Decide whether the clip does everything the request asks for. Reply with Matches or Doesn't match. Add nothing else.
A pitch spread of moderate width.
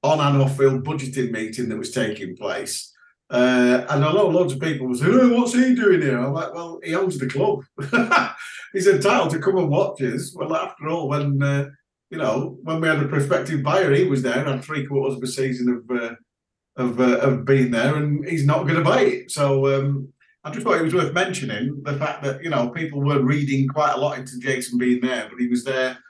Matches